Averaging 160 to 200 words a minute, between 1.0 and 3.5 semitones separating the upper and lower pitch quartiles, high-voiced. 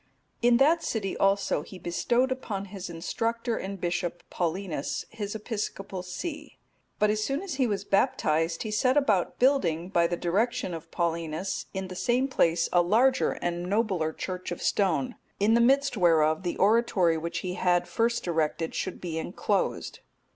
No: average, 165 wpm; average, 5.1 semitones; high, 195 Hz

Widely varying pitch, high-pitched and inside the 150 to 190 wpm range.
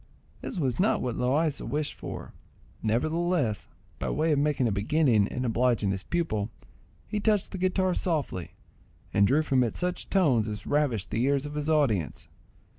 No: wide, 6.1 semitones; medium, 140 Hz; average, 170 wpm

